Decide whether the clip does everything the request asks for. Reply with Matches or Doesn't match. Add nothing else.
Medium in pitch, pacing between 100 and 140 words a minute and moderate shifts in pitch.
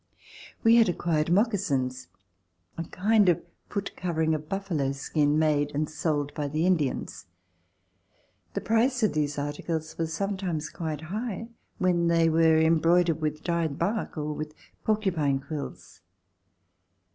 Matches